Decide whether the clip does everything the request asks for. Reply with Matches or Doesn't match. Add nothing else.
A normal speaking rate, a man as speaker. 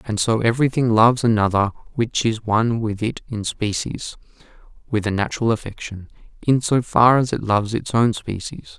Matches